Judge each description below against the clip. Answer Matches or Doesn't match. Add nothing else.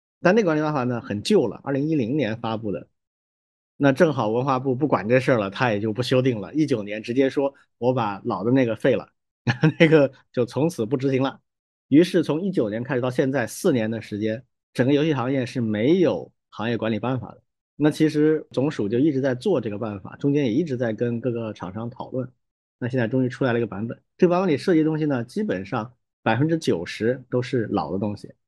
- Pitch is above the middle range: Doesn't match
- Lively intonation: Doesn't match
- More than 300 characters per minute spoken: Matches